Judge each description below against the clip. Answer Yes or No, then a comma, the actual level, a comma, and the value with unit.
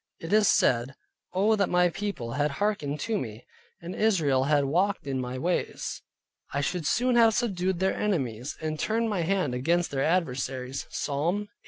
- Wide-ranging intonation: Yes, wide, 6.6 semitones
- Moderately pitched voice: Yes, medium, 170 Hz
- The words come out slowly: No, average, 175 wpm